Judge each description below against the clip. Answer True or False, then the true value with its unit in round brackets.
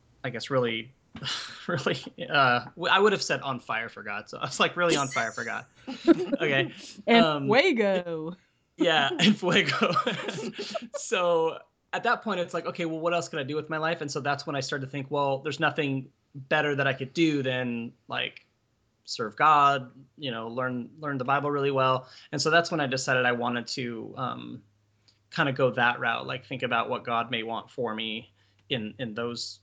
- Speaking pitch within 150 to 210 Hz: False (140 Hz)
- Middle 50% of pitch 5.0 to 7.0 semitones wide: True (5.3 semitones)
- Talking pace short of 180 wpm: False (205 wpm)